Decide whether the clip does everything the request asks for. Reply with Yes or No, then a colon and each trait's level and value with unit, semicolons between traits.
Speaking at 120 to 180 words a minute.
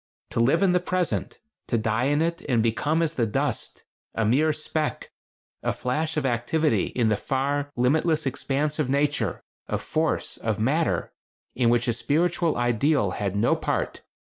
Yes: average, 165 wpm